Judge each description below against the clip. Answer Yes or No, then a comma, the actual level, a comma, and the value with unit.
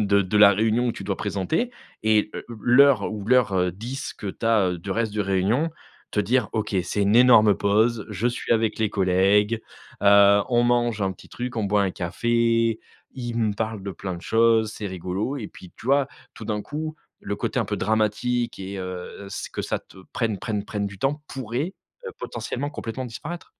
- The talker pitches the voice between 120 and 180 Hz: No, low, 110 Hz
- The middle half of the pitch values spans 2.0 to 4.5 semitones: Yes, average, 3.0 semitones